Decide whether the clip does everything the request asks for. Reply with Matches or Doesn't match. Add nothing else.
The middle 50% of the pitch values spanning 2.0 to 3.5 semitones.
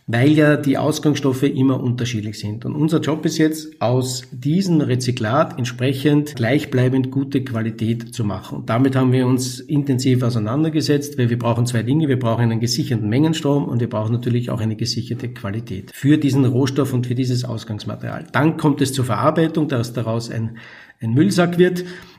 Doesn't match